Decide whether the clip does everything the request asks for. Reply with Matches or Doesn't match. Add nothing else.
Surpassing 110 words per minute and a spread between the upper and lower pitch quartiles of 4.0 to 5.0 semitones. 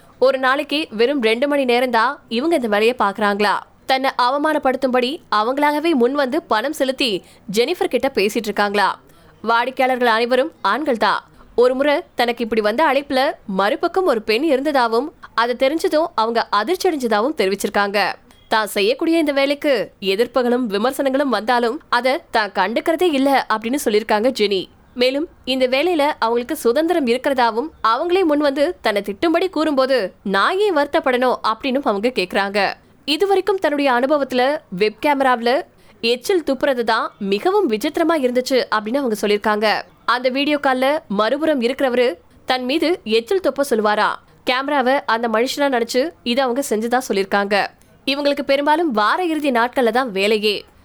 Matches